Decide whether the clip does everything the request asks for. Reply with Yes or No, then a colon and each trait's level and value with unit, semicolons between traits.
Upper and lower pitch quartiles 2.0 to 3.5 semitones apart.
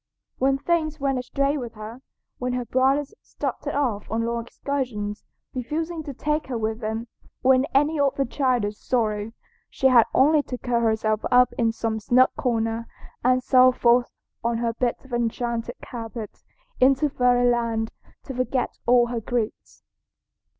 Yes: narrow, 2.6 semitones